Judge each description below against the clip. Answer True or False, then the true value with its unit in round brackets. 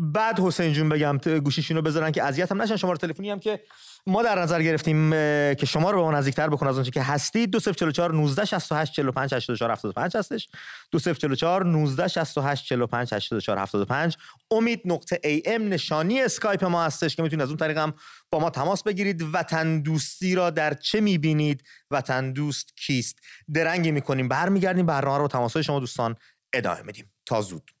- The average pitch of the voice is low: False (155 Hz)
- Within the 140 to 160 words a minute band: True (155 wpm)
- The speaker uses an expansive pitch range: False (3.9 semitones)